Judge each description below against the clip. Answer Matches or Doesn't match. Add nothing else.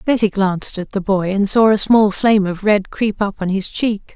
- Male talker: Doesn't match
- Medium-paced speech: Doesn't match